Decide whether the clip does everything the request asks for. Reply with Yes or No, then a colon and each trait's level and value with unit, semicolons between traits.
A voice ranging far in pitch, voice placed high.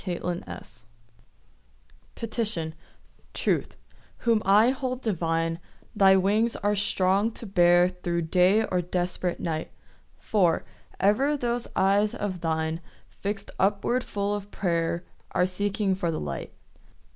No: average, 3.2 semitones; high, 195 Hz